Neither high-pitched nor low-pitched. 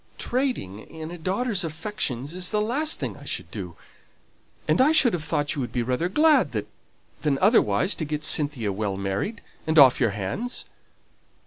Yes: medium, 160 Hz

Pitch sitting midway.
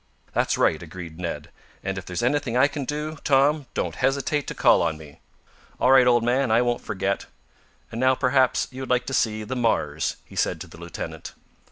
No: low, 125 Hz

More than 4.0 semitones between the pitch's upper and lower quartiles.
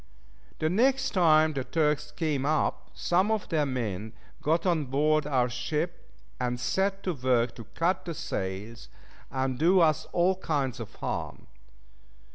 Yes: average, 5.3 semitones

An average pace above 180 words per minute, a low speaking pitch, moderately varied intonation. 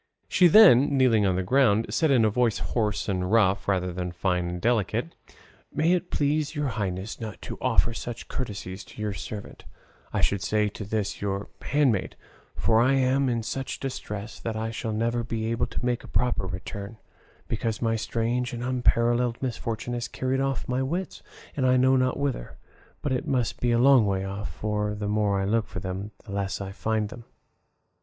Yes: average, 195 wpm; low, 115 Hz; average, 3.9 semitones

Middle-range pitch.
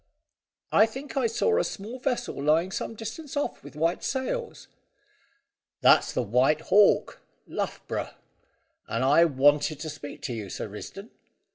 Yes: medium, 170 Hz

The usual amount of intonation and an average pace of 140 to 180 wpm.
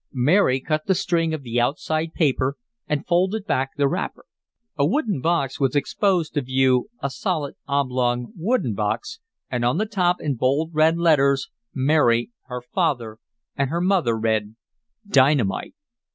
Yes: average, 5.0 semitones; average, 150 wpm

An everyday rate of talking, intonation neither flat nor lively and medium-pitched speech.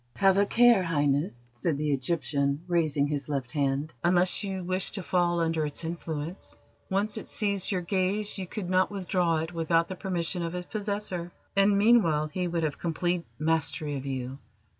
Yes: average, 180 wpm; average, 3.8 semitones; medium, 170 Hz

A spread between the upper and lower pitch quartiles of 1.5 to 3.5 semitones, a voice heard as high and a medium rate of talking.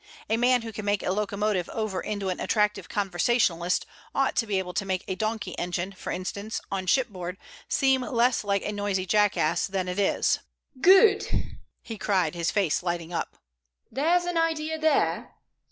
No: average, 4.4 semitones; high, 205 Hz; average, 170 wpm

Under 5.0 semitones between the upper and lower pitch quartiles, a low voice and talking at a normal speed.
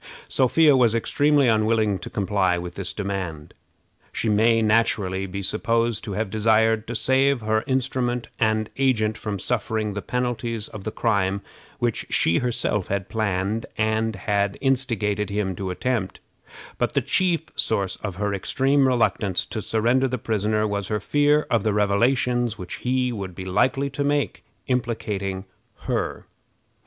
Yes: average, 3.5 semitones; low, 110 Hz; average, 150 wpm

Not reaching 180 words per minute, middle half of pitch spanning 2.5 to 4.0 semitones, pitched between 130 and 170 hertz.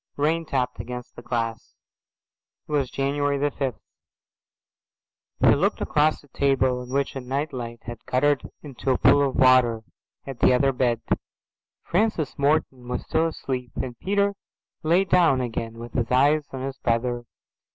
Yes: average, 160 wpm; average, 2.8 semitones; low, 135 Hz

